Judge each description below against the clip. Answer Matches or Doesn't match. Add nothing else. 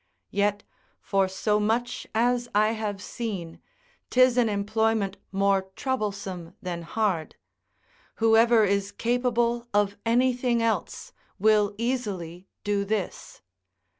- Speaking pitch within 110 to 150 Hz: Doesn't match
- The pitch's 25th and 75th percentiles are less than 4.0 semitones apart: Matches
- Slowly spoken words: Matches